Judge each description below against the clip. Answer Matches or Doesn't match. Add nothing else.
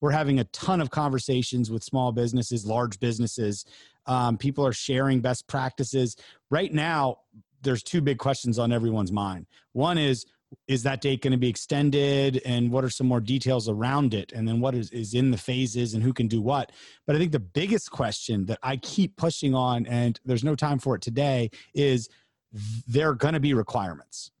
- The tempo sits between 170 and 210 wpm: Matches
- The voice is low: Matches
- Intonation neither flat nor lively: Matches